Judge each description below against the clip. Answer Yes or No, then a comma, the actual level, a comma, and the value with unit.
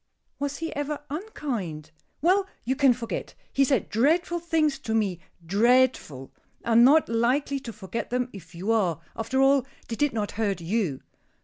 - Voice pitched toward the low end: No, high, 240 Hz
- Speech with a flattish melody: No, wide, 5.5 semitones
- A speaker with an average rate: Yes, average, 170 wpm